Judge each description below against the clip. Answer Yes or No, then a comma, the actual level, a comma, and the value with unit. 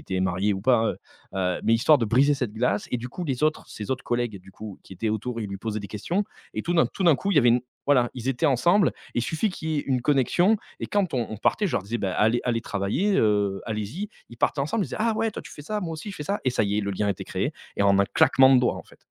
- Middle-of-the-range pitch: No, low, 120 Hz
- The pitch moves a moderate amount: No, wide, 6.8 semitones